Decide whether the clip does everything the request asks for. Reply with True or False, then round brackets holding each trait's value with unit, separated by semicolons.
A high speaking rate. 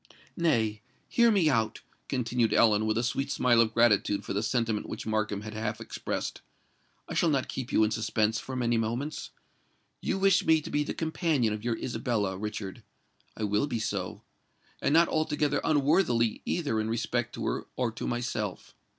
False (170 wpm)